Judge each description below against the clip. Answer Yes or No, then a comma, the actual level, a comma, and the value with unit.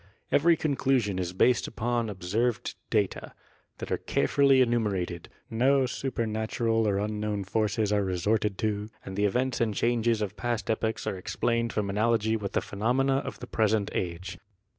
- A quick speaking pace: No, average, 155 wpm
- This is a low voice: Yes, low, 110 Hz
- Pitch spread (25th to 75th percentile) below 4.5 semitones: Yes, average, 2.9 semitones